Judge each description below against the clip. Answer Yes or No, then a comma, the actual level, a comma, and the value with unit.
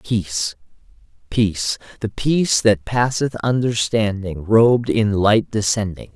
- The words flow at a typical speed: No, slow, 100 wpm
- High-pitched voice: No, low, 110 Hz